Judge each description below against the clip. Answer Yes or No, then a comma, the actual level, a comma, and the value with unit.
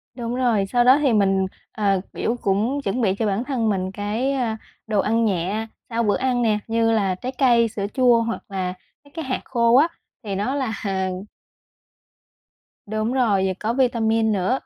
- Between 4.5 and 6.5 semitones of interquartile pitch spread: No, average, 3.4 semitones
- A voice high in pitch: Yes, high, 225 Hz